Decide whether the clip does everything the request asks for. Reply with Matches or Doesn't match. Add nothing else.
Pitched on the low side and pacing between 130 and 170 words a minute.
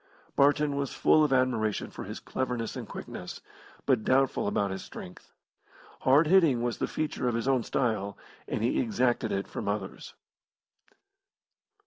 Matches